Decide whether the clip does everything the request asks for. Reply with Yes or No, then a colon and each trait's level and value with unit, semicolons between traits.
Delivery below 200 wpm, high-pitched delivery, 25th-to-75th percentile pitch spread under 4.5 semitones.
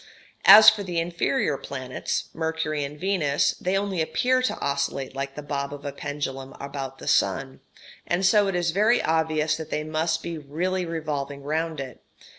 No: average, 175 wpm; medium, 155 Hz; average, 3.7 semitones